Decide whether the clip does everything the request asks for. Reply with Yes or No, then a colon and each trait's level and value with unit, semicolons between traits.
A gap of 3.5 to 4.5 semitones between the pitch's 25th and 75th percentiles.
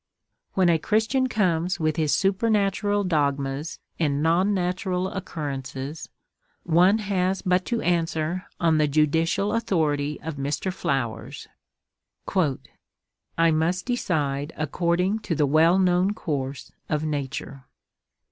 Yes: average, 4.1 semitones